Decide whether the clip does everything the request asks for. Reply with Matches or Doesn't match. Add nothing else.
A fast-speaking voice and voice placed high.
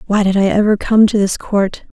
Matches